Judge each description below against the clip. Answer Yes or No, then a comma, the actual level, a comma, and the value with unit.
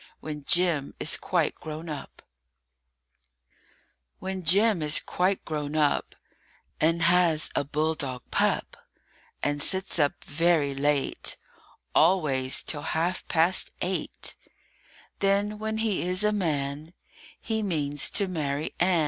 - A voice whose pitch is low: No, medium, 160 Hz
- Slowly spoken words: Yes, slow, 120 wpm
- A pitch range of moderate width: Yes, average, 4.0 semitones